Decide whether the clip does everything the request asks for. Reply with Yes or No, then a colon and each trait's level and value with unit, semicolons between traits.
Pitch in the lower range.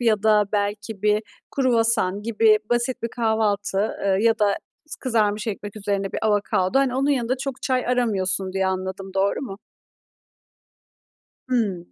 No: high, 215 Hz